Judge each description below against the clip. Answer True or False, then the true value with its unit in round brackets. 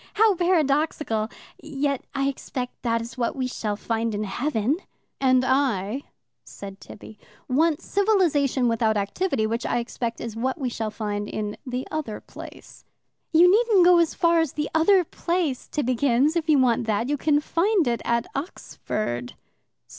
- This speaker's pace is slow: False (160 wpm)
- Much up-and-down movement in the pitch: True (5.7 semitones)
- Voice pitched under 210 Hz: False (260 Hz)